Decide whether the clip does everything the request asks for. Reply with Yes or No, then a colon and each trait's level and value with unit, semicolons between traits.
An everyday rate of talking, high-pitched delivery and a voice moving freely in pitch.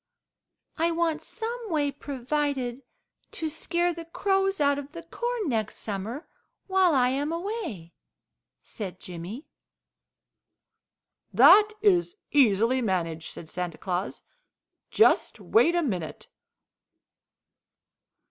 No: slow, 105 wpm; very high, 290 Hz; wide, 8.2 semitones